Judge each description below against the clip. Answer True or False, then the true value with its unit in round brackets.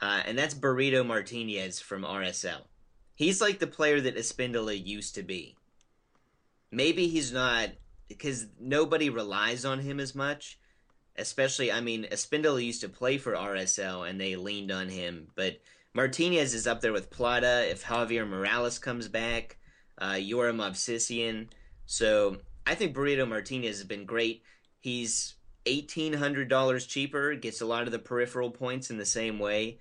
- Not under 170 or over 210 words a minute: False (160 wpm)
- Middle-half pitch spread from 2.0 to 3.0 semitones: False (3.9 semitones)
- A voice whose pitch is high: False (120 Hz)